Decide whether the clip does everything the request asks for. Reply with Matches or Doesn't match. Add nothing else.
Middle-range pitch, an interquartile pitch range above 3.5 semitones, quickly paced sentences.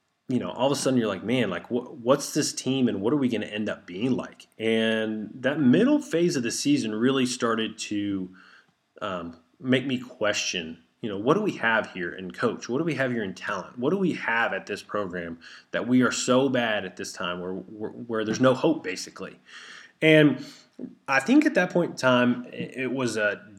Doesn't match